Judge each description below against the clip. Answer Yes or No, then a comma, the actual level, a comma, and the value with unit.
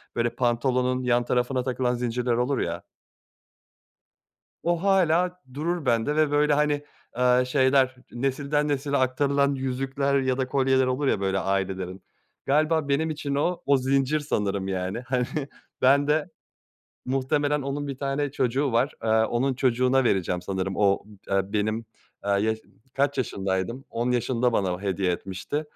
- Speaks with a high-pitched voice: No, low, 130 Hz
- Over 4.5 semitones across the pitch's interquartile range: No, average, 3.6 semitones